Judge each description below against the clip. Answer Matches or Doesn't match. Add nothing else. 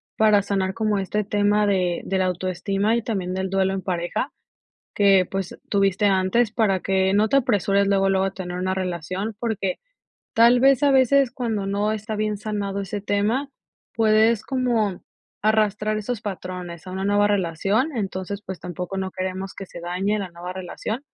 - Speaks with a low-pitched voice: Doesn't match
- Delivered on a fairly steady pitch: Matches